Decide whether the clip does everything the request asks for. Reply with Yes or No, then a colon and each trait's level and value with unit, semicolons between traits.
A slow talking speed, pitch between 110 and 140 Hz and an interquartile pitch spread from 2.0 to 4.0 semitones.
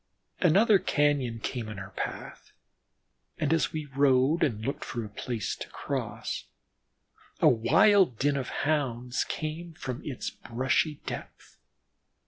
No: slow, 130 wpm; low, 135 Hz; average, 4.5 semitones